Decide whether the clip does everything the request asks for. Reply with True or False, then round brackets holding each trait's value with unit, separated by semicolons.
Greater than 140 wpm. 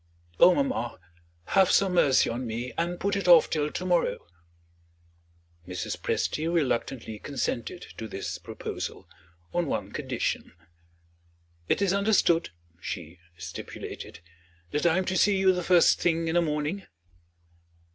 False (135 wpm)